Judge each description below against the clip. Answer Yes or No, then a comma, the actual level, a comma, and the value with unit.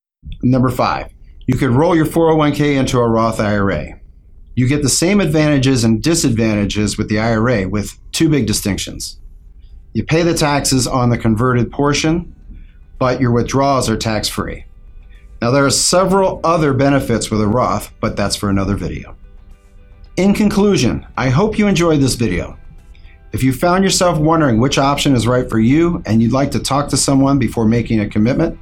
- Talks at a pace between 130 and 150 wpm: No, average, 175 wpm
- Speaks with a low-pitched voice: Yes, low, 120 Hz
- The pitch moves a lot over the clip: Yes, wide, 5.9 semitones